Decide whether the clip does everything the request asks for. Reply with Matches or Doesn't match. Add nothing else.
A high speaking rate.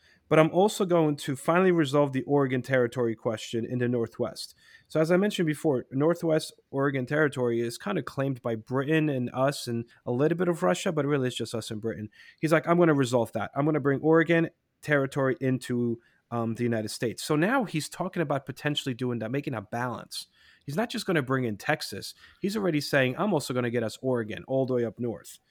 Matches